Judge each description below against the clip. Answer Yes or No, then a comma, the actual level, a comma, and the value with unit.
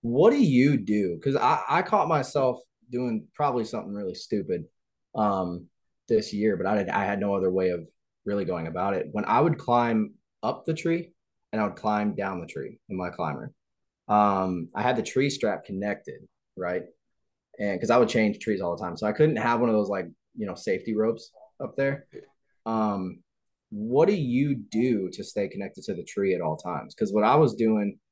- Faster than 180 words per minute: Yes, fast, 205 wpm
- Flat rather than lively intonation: No, average, 4.3 semitones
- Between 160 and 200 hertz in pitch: No, low, 110 Hz